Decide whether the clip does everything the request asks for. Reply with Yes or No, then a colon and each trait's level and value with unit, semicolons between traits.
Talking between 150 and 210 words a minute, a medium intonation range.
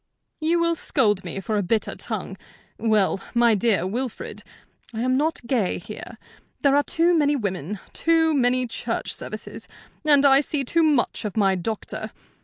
No: average, 165 wpm; wide, 5.9 semitones